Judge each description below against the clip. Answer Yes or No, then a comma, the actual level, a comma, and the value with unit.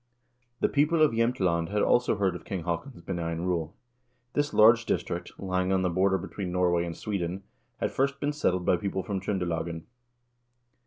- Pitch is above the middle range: No, very low, 95 Hz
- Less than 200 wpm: Yes, average, 170 wpm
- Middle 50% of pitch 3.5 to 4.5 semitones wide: Yes, average, 3.9 semitones